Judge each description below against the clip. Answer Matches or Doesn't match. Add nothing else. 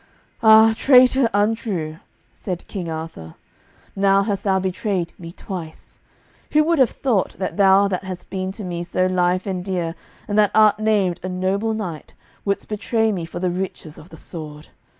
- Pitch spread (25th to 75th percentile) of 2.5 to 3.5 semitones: Matches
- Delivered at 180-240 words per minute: Doesn't match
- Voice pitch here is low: Doesn't match